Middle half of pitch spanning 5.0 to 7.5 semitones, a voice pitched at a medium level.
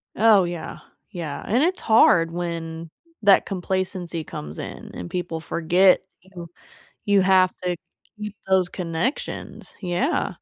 No: narrow, 2.6 semitones; medium, 180 Hz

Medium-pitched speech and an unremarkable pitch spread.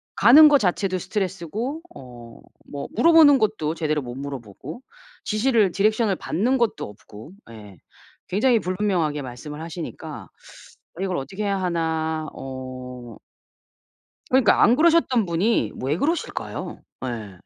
No: medium, 175 Hz; wide, 8.5 semitones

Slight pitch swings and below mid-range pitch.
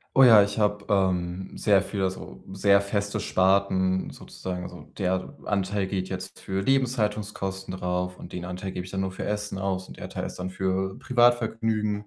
Yes: narrow, 1.9 semitones; very low, 95 Hz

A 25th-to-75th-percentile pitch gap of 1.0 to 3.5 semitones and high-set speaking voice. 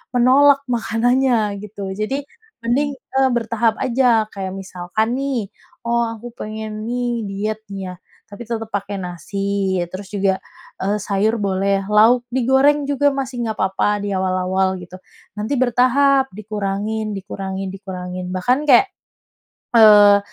No: average, 3.9 semitones; high, 215 Hz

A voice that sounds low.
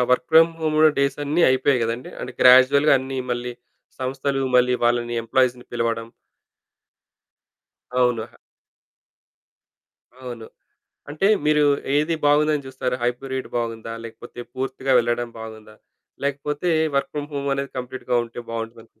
Yes: low, 130 Hz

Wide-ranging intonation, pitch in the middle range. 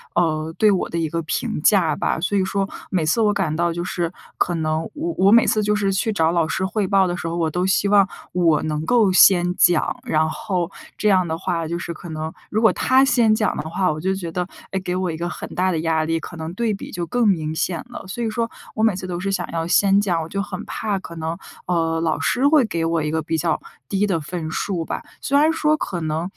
No: average, 3.7 semitones; medium, 180 Hz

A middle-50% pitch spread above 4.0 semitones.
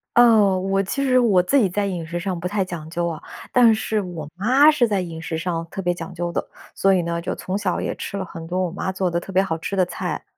No: average, 2.9 semitones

